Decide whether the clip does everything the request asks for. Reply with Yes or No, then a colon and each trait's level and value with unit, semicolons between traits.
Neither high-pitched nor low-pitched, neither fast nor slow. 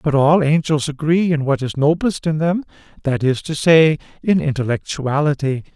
Yes: medium, 150 Hz; average, 155 wpm